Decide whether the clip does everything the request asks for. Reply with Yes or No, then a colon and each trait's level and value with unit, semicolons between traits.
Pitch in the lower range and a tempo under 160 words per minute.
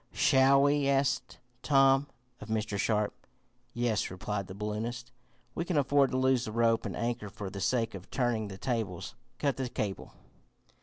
No: low, 120 Hz; average, 165 wpm